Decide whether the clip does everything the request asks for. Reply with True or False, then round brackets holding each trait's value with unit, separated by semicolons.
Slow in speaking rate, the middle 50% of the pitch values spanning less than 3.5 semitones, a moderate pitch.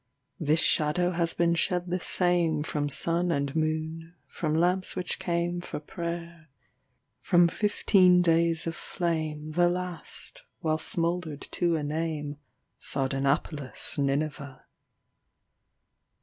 True (90 wpm; 2.6 semitones; 165 Hz)